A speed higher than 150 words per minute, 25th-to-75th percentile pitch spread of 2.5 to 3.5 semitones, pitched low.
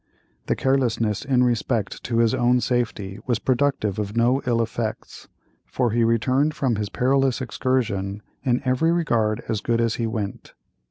Yes: average, 160 wpm; average, 2.8 semitones; low, 120 Hz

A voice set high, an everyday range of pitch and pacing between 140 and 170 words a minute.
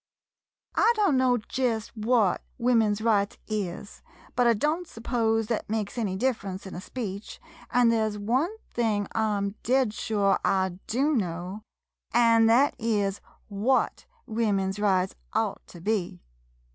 Yes: high, 220 Hz; average, 3.1 semitones; average, 150 wpm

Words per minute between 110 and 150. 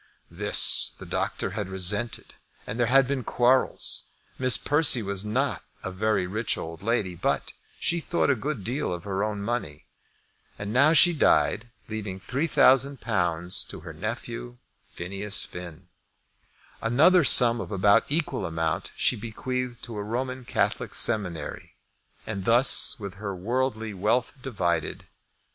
Yes: average, 140 wpm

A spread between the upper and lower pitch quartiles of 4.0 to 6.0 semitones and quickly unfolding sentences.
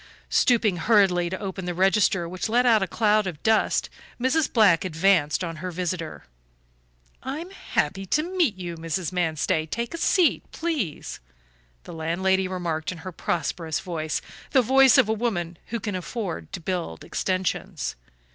No: average, 4.6 semitones; average, 155 wpm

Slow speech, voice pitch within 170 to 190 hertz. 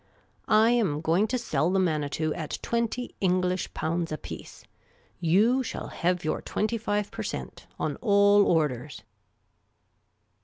Yes: slow, 130 wpm; medium, 185 Hz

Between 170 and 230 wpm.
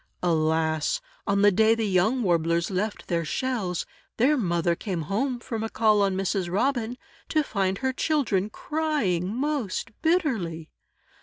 No: average, 145 wpm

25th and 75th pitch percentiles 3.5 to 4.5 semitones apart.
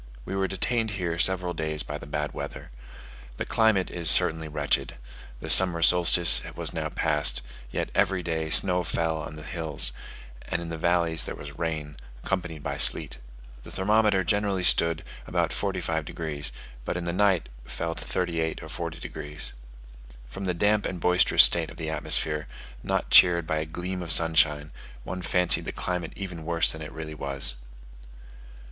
No: narrow, 2.6 semitones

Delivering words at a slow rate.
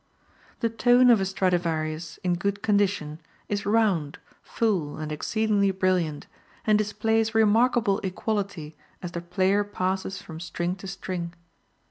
Yes: slow, 130 wpm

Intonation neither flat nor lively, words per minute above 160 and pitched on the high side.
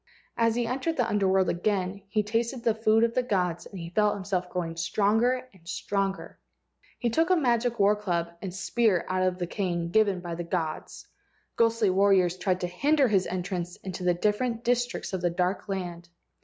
Yes: average, 4.2 semitones; average, 195 wpm; high, 195 Hz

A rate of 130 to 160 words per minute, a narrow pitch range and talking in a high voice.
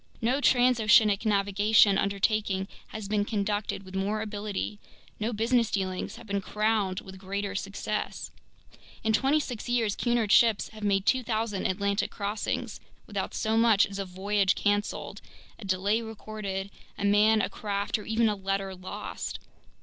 Yes: average, 150 wpm; narrow, 1.9 semitones; high, 205 Hz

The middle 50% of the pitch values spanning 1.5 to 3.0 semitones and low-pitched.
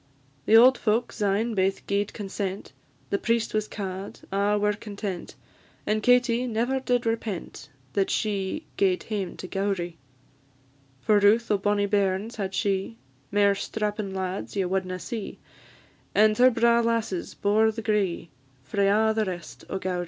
No: narrow, 2.4 semitones; high, 205 Hz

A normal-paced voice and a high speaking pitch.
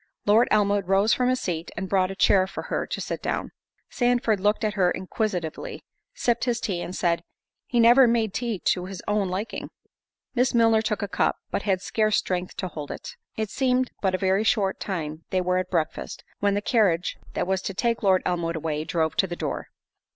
No: fast, 210 wpm; high, 195 Hz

